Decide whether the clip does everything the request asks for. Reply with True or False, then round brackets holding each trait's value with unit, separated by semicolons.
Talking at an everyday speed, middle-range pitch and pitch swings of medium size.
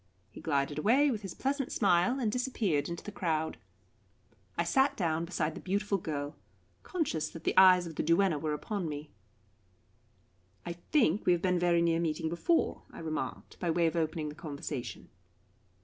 True (175 wpm; 170 Hz; 4.3 semitones)